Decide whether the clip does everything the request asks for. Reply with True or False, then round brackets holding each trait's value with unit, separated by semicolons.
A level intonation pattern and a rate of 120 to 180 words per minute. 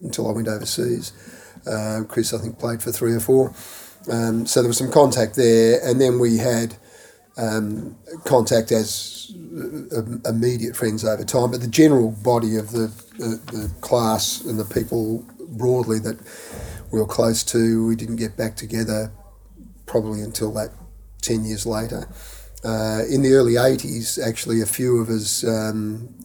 True (1.4 semitones; 165 wpm)